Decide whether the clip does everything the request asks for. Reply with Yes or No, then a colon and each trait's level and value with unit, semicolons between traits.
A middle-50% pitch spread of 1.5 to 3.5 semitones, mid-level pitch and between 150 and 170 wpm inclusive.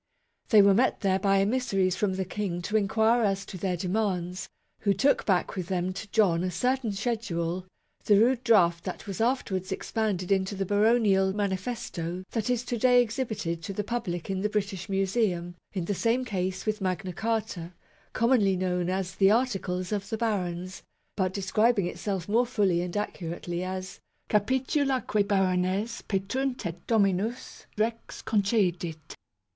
No: average, 3.2 semitones; high, 195 Hz; average, 160 wpm